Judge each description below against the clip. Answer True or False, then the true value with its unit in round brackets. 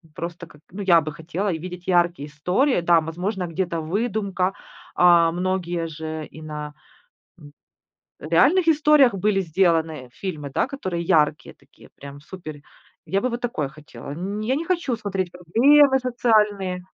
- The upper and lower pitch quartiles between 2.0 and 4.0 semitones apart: False (4.6 semitones)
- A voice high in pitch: False (180 Hz)